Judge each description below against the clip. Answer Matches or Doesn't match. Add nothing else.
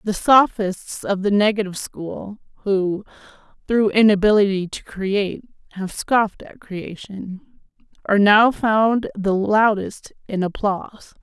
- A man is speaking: Doesn't match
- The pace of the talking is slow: Matches